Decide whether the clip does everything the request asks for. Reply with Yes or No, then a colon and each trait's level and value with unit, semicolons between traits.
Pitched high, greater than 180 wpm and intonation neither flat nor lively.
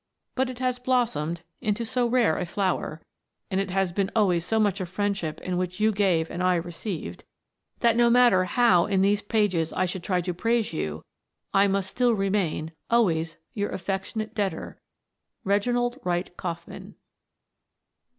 No: high, 195 Hz; average, 160 wpm; average, 4.2 semitones